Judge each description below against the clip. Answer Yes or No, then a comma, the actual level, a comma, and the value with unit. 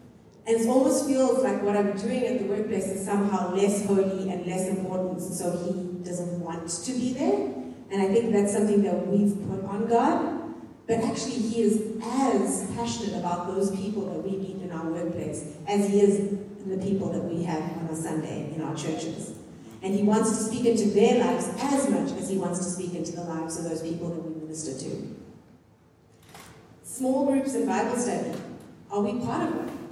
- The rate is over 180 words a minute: Yes, average, 200 wpm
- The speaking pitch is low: No, high, 200 Hz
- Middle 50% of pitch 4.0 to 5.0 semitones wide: Yes, average, 4.5 semitones